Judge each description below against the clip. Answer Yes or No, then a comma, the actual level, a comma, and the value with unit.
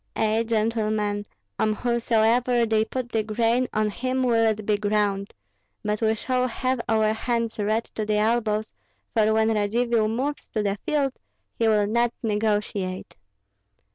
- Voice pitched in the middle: No, high, 220 Hz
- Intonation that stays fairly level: Yes, narrow, 1.9 semitones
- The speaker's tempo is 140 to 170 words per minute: Yes, average, 150 wpm